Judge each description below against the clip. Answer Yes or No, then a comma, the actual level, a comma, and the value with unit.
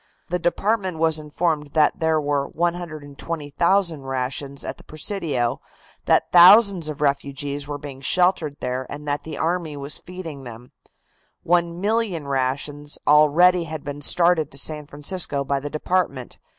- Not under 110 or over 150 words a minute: Yes, average, 145 wpm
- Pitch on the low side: No, medium, 150 Hz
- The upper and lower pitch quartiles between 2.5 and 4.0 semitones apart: Yes, average, 3.5 semitones